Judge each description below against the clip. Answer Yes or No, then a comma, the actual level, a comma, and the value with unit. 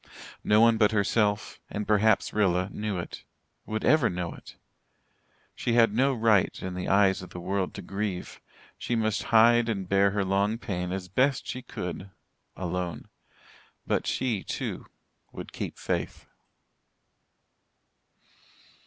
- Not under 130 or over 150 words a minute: Yes, average, 140 wpm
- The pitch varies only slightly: No, average, 3.3 semitones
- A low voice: Yes, low, 105 Hz